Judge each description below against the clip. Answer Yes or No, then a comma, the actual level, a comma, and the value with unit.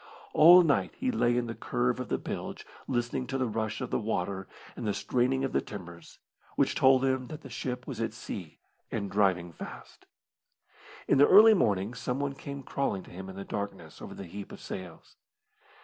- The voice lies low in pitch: Yes, low, 120 Hz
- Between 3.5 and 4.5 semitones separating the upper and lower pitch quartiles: No, wide, 5.5 semitones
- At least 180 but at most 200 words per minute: Yes, average, 195 wpm